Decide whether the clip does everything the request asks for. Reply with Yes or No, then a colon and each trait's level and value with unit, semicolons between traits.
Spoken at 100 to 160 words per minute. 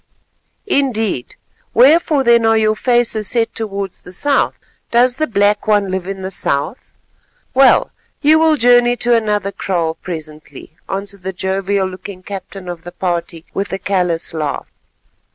Yes: average, 150 wpm